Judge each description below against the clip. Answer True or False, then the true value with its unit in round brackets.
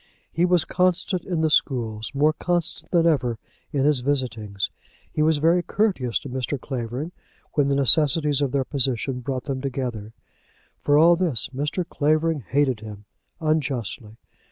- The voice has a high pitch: False (140 Hz)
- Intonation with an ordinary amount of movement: True (4.3 semitones)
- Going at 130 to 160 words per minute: True (155 wpm)